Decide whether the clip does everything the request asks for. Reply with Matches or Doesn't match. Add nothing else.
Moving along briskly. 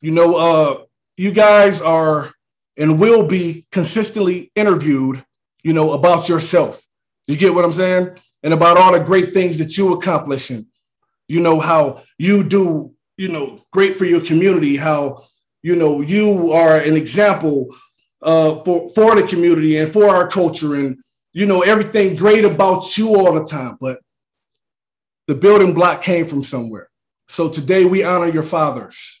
Doesn't match